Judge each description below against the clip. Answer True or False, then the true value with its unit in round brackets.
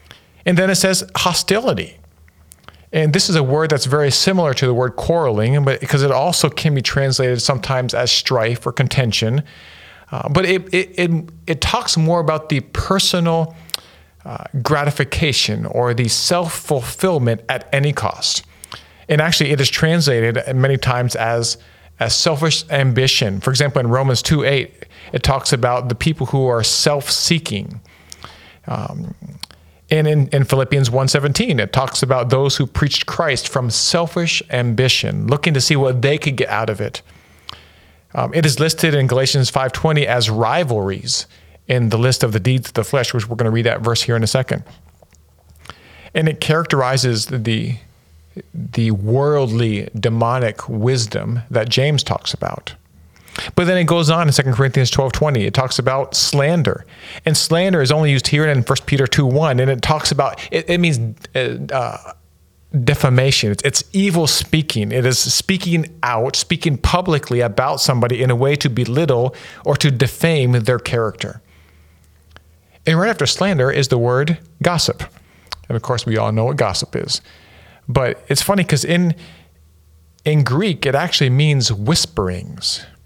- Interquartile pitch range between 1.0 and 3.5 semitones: False (5.0 semitones)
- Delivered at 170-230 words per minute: False (160 wpm)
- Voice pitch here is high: False (135 Hz)